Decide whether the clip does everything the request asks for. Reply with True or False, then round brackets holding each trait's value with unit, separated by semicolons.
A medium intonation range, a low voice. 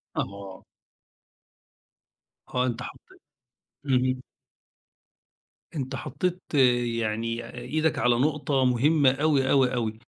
True (3.3 semitones; 130 Hz)